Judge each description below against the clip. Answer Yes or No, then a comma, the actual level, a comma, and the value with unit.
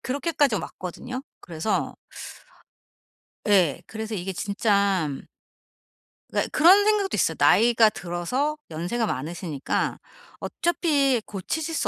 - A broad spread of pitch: Yes, wide, 8.0 semitones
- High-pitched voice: Yes, high, 220 Hz